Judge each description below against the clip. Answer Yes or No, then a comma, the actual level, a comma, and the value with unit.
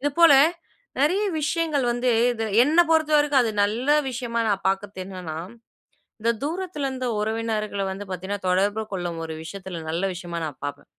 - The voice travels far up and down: Yes, wide, 6.9 semitones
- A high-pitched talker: Yes, high, 220 Hz